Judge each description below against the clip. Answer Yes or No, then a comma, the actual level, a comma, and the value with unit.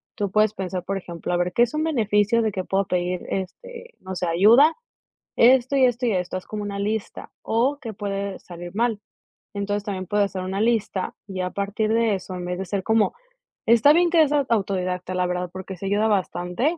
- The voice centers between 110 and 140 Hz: No, high, 200 Hz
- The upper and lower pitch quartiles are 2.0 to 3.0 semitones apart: No, average, 3.8 semitones